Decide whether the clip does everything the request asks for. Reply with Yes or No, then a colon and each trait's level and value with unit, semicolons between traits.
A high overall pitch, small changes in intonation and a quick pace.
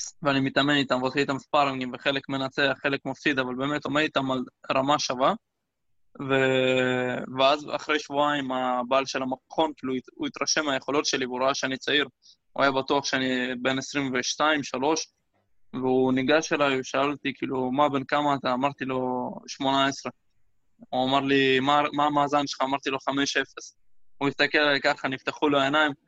No: low, 135 Hz; narrow, 1.7 semitones; fast, 155 wpm